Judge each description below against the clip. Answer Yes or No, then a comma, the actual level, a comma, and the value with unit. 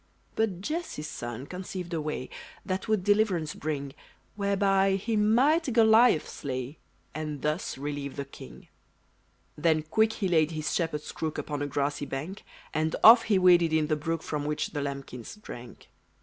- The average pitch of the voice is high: No, medium, 160 Hz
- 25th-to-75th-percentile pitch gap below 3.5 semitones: No, average, 5.3 semitones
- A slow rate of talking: No, average, 160 wpm